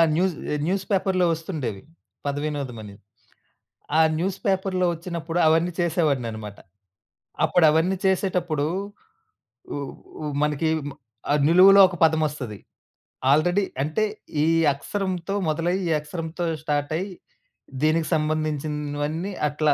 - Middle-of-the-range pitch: Yes, medium, 160 Hz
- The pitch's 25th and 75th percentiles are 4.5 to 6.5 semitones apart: No, average, 3.4 semitones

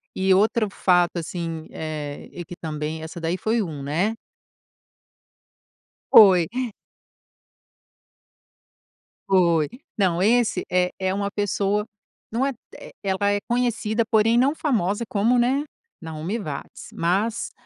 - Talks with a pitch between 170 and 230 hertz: Yes, high, 190 Hz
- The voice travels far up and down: No, average, 4.6 semitones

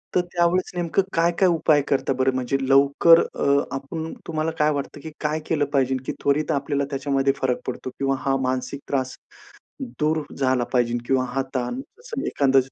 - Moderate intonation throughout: Yes, average, 3.0 semitones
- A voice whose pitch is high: No, medium, 140 Hz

